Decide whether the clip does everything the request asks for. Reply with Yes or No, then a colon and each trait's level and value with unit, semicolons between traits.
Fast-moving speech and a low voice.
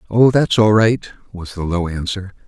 No: average, 195 wpm; low, 100 Hz